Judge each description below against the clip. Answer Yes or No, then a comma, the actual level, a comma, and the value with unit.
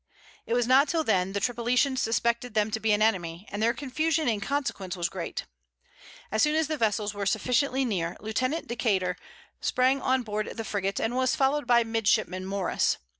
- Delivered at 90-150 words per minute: No, average, 185 wpm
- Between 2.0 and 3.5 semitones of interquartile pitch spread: No, average, 4.1 semitones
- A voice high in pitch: Yes, high, 225 Hz